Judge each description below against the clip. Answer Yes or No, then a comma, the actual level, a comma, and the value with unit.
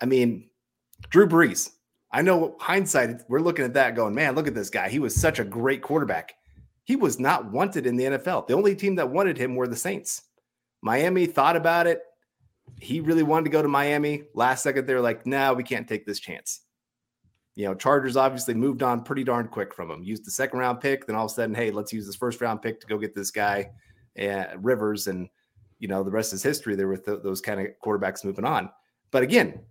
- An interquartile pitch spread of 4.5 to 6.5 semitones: Yes, average, 4.8 semitones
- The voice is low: Yes, low, 125 Hz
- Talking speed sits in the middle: No, fast, 230 wpm